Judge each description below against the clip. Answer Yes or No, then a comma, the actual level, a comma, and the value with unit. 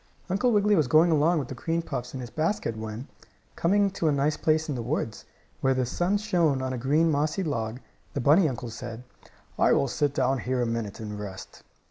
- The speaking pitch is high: No, medium, 140 Hz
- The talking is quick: Yes, fast, 215 wpm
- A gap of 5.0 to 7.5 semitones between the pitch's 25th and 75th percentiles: Yes, average, 5.3 semitones